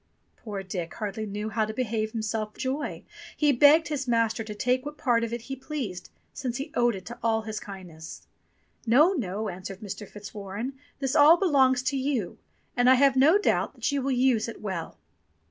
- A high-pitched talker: Yes, high, 230 Hz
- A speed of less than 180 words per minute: No, average, 195 wpm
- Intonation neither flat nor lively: Yes, average, 4.3 semitones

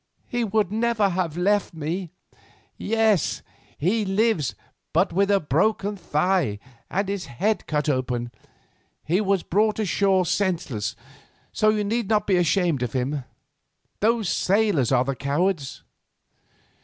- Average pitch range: No, wide, 5.8 semitones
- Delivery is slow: Yes, slow, 130 wpm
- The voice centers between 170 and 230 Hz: Yes, high, 190 Hz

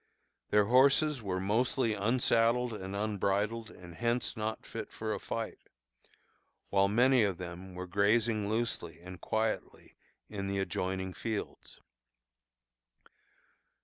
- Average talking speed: No, slow, 115 wpm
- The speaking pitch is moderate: No, low, 105 Hz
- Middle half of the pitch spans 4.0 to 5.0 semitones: No, average, 3.4 semitones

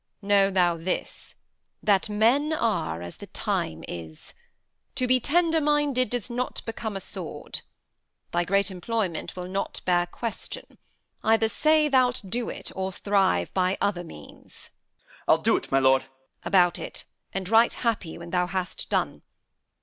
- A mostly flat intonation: No, average, 5.2 semitones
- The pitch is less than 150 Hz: No, high, 195 Hz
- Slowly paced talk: No, average, 150 wpm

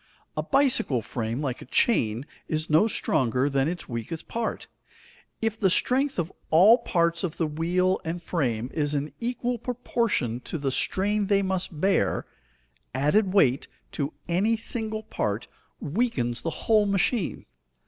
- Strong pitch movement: Yes, wide, 7.5 semitones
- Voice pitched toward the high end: No, medium, 170 Hz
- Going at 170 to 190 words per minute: No, average, 150 wpm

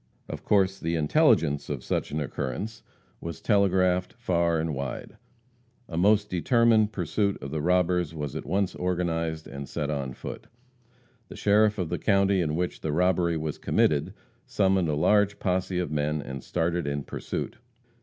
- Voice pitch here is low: Yes, very low, 85 Hz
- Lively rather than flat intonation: No, average, 4.0 semitones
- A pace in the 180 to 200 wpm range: No, average, 165 wpm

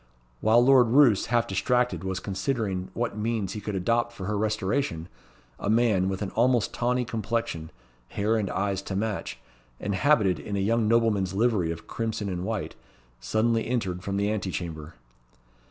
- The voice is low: Yes, low, 105 Hz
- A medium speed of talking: Yes, average, 170 wpm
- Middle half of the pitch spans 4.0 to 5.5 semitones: No, average, 3.5 semitones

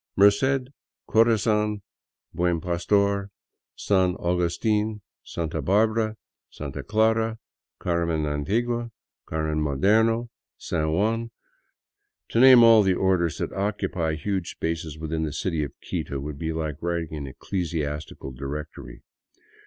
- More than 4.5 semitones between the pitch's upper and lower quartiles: Yes, wide, 5.5 semitones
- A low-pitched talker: Yes, very low, 90 Hz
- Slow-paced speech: Yes, slow, 115 wpm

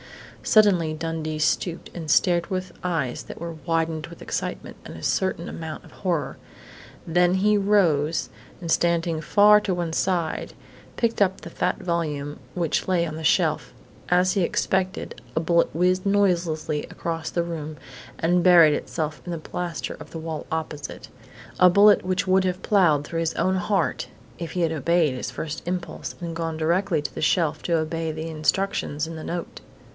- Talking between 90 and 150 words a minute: No, average, 175 wpm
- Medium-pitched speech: Yes, medium, 170 Hz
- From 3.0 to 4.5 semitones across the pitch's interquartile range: No, narrow, 2.5 semitones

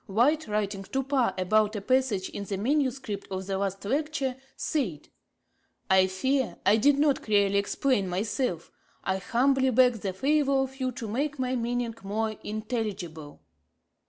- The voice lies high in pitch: Yes, high, 225 Hz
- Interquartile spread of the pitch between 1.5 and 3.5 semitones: No, average, 5.1 semitones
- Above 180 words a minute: No, average, 155 wpm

